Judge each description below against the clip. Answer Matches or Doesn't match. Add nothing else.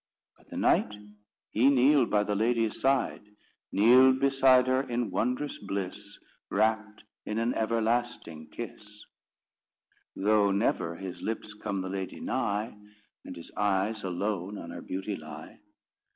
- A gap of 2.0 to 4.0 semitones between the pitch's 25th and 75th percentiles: Matches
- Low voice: Matches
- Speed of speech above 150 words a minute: Doesn't match